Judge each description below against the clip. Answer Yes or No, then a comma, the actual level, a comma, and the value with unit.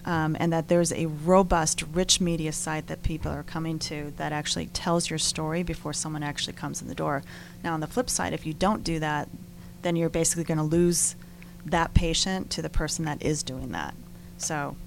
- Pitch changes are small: Yes, narrow, 1.8 semitones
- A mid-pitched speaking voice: Yes, medium, 165 Hz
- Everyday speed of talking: No, fast, 210 wpm